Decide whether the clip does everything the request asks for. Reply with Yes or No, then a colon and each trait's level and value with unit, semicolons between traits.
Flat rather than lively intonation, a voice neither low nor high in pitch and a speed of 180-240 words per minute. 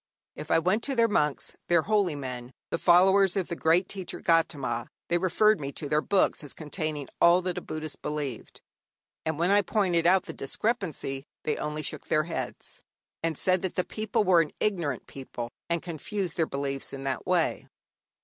No: average, 4.2 semitones; medium, 165 Hz; average, 190 wpm